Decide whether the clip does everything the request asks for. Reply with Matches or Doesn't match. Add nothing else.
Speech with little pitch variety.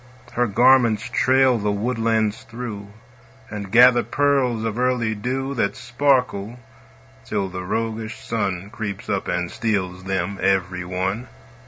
Doesn't match